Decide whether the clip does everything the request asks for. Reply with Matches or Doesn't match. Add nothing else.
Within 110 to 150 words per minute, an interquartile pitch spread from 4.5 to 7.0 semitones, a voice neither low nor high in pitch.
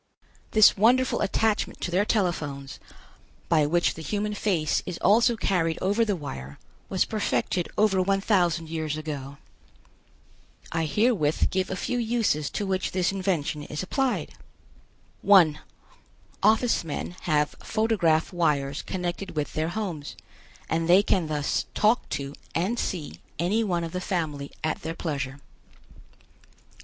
Matches